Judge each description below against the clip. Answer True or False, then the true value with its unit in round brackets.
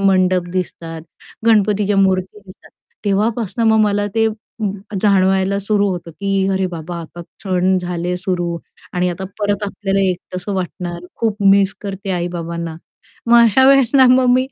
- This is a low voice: False (190 Hz)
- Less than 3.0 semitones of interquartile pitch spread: True (2.4 semitones)